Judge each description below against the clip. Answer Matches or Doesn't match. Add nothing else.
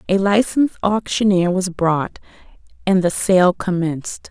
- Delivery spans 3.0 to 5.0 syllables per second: Matches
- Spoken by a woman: Matches